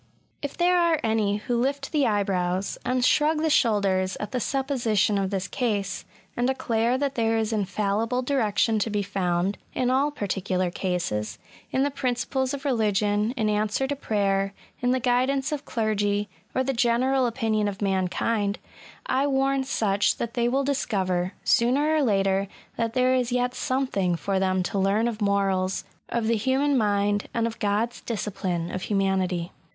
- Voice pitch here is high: Yes, high, 220 Hz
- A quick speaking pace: No, average, 170 wpm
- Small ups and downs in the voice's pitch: No, average, 4.6 semitones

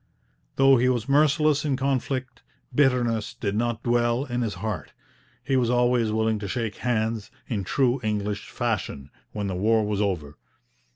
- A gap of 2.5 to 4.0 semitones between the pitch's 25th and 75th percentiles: Yes, average, 3.3 semitones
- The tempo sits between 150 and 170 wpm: Yes, average, 160 wpm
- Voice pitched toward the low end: Yes, low, 120 Hz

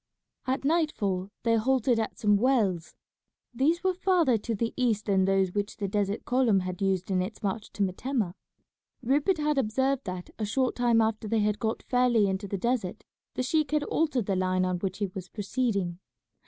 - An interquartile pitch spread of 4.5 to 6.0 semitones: Yes, average, 5.0 semitones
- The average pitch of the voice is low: No, high, 220 Hz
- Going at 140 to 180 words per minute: No, average, 190 wpm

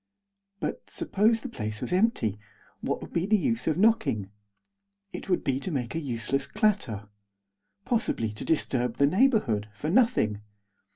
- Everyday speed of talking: Yes, average, 155 wpm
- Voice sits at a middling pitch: Yes, medium, 150 Hz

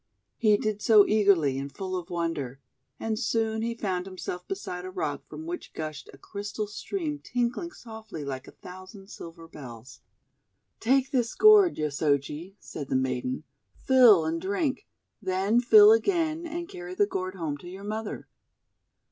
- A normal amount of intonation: No, wide, 6.1 semitones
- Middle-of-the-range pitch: No, high, 195 Hz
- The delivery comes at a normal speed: Yes, average, 155 wpm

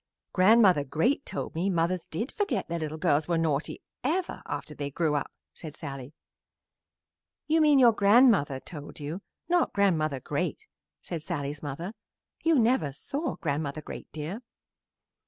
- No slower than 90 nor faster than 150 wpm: Yes, average, 145 wpm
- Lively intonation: Yes, wide, 7.2 semitones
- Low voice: No, medium, 165 Hz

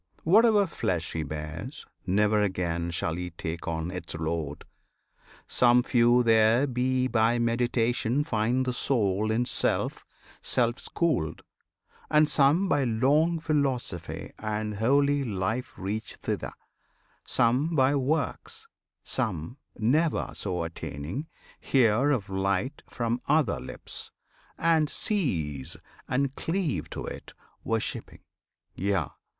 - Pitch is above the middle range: No, low, 120 Hz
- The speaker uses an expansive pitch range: Yes, wide, 6.7 semitones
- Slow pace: Yes, slow, 115 wpm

